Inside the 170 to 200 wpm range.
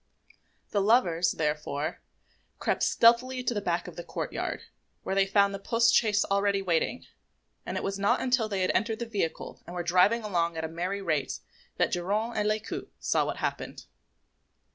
Yes: average, 185 wpm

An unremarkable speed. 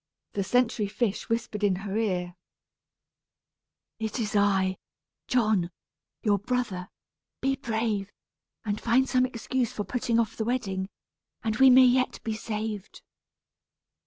No: slow, 130 wpm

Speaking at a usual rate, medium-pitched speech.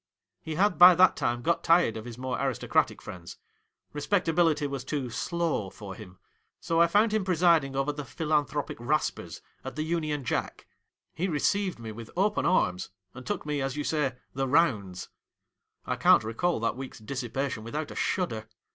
Yes: average, 180 wpm; medium, 145 Hz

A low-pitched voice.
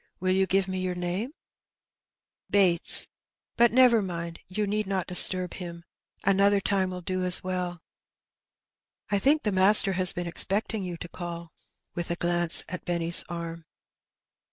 No: medium, 185 Hz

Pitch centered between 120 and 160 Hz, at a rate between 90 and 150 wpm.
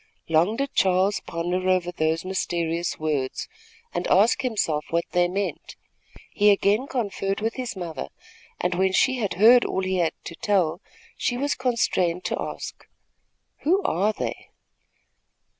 No: high, 190 Hz; average, 145 wpm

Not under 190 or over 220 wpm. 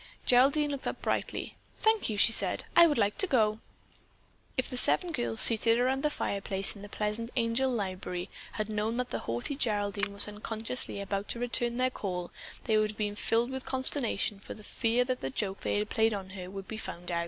Yes: average, 200 wpm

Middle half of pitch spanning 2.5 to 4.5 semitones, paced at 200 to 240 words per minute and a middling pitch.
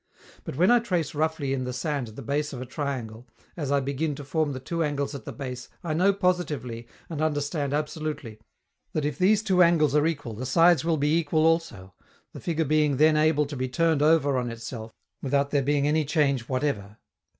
Yes: average, 3.3 semitones; fast, 205 wpm; medium, 145 Hz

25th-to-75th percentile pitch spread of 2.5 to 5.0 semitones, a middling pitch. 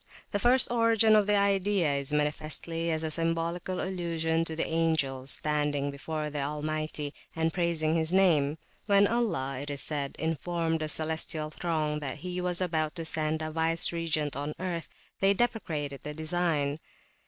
Yes: average, 2.8 semitones; medium, 160 Hz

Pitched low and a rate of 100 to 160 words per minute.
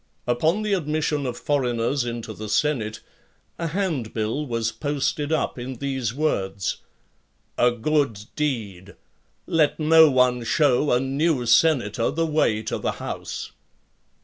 Yes: low, 130 Hz; slow, 135 wpm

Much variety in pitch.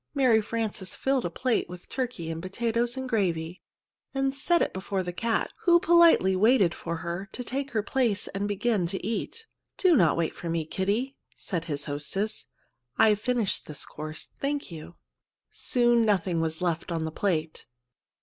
Yes: wide, 6.4 semitones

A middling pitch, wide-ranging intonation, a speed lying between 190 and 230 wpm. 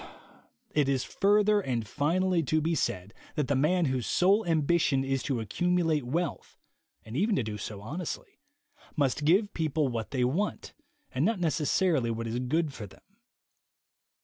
No: medium, 150 Hz; wide, 5.8 semitones; average, 160 wpm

